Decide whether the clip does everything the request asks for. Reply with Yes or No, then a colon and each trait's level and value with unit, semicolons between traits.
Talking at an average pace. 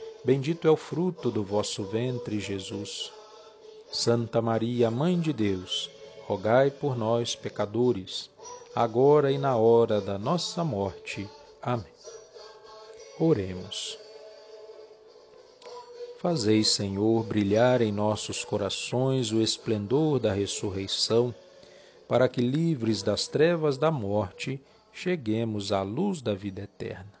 No: slow, 110 wpm